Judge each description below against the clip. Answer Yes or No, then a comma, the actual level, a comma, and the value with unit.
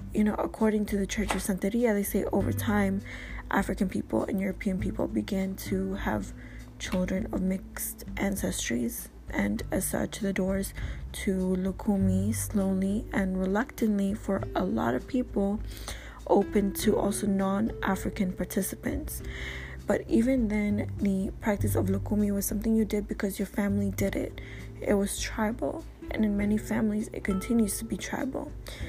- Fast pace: No, average, 150 wpm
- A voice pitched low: No, high, 195 Hz